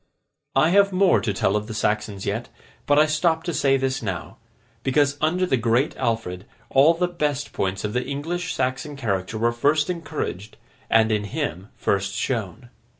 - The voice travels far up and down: Yes, wide, 6.4 semitones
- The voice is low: Yes, low, 130 Hz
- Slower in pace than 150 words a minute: No, average, 175 wpm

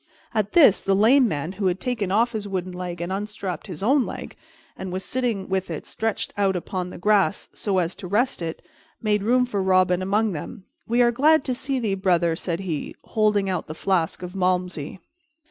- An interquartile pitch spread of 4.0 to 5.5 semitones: No, average, 3.3 semitones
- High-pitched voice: Yes, high, 195 Hz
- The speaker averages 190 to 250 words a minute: Yes, fast, 205 wpm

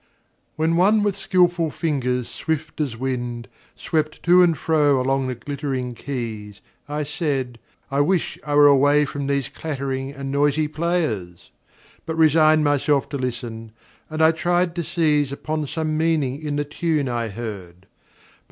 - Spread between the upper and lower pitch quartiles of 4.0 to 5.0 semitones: No, average, 3.6 semitones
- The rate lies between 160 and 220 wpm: No, average, 150 wpm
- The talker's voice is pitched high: No, medium, 145 Hz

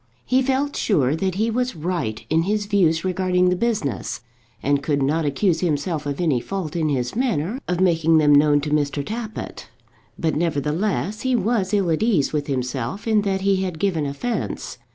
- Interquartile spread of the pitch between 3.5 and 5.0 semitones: No, wide, 5.5 semitones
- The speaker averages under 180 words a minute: No, average, 185 wpm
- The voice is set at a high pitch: No, medium, 170 Hz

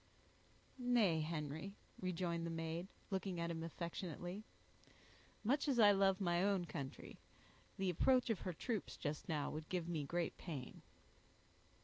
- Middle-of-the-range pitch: Yes, medium, 175 Hz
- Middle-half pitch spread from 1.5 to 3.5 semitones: Yes, average, 3.2 semitones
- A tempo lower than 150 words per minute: Yes, average, 140 wpm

